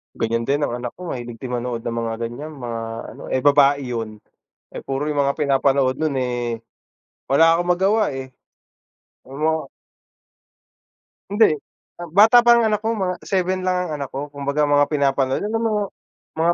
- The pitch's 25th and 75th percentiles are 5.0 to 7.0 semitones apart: Yes, wide, 5.6 semitones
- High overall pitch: No, medium, 140 Hz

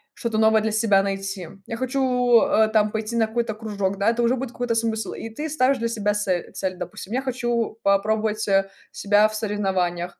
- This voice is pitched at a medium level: No, high, 220 Hz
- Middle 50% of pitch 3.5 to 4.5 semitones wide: No, average, 2.7 semitones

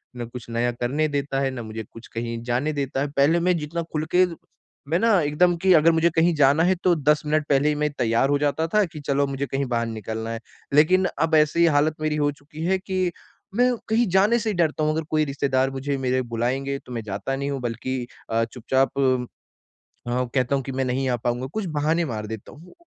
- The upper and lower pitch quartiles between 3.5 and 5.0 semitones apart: Yes, average, 4.0 semitones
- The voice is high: No, medium, 140 Hz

